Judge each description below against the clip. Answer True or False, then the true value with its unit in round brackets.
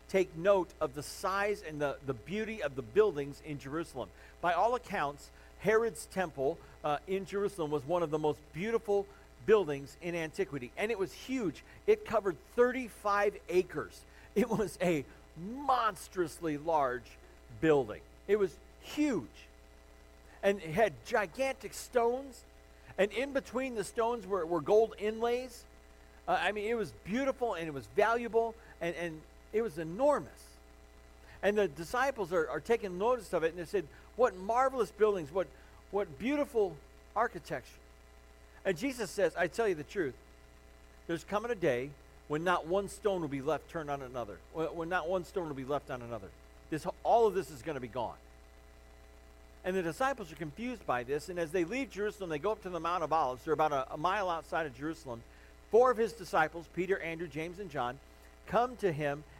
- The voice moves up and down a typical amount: False (7.4 semitones)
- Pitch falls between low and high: True (175 Hz)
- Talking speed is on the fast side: False (180 wpm)